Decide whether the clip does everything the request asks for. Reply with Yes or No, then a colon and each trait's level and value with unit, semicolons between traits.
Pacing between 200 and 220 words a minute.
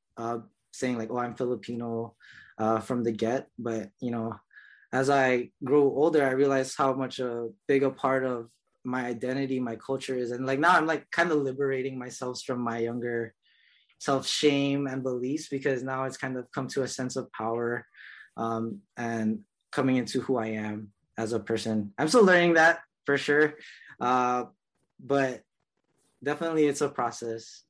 No: average, 170 wpm